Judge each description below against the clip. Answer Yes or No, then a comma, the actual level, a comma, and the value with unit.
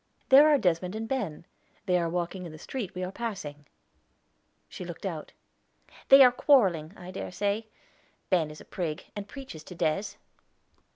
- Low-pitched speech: No, medium, 185 Hz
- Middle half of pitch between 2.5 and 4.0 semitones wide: No, average, 5.1 semitones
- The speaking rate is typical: Yes, average, 170 wpm